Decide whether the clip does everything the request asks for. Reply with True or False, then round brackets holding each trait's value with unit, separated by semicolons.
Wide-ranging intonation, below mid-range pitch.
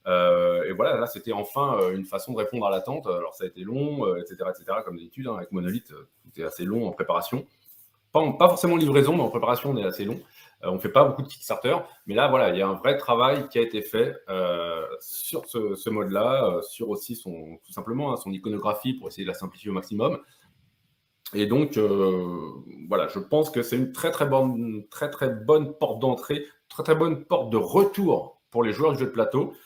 True (6.6 semitones; 125 Hz)